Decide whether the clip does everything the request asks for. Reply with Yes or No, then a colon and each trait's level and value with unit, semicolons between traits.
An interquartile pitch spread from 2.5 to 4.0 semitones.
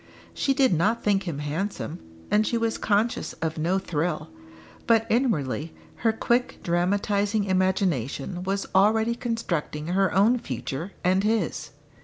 No: average, 4.6 semitones